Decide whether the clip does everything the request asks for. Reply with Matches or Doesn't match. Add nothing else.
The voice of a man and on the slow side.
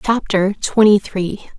Doesn't match